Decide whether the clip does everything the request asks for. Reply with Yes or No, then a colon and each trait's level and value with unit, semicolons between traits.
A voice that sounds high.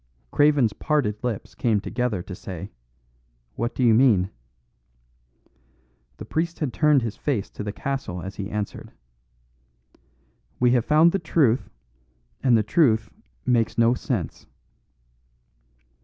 No: low, 120 Hz